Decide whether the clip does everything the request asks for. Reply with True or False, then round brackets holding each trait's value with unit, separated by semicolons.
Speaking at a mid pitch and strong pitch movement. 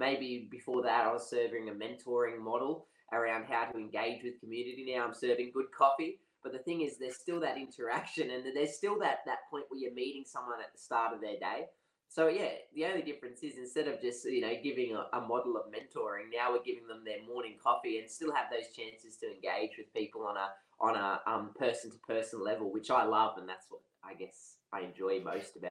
False (130 Hz; 8.3 semitones)